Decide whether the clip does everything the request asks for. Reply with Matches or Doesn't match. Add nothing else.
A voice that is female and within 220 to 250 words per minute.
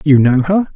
Doesn't match